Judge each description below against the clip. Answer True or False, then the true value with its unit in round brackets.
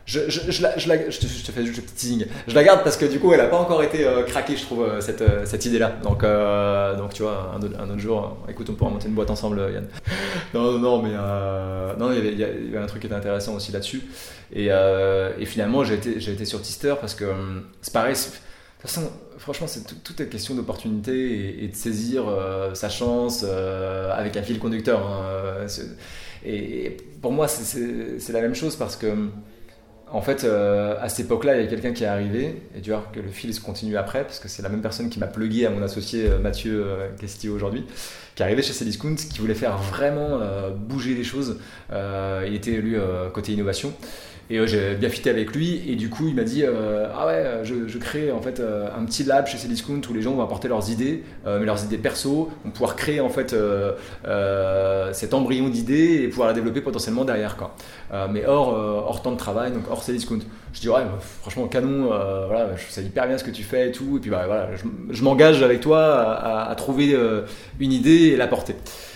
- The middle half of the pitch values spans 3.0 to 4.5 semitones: True (3.6 semitones)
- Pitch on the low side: True (110 Hz)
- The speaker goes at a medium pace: False (240 wpm)